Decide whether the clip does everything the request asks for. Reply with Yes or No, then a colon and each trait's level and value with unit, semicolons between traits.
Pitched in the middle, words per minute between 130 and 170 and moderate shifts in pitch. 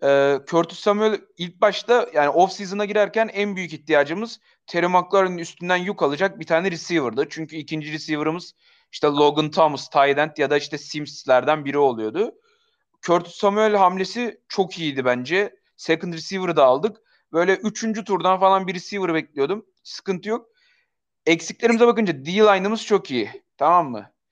Yes: medium, 180 Hz; fast, 140 wpm; average, 4.9 semitones